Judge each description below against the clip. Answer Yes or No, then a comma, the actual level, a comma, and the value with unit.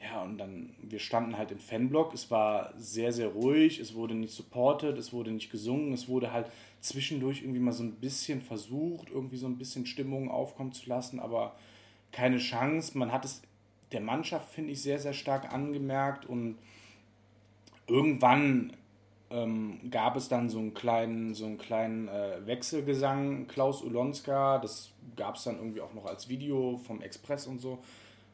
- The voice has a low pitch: Yes, low, 125 Hz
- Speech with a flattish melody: No, average, 3.4 semitones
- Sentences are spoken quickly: No, average, 175 wpm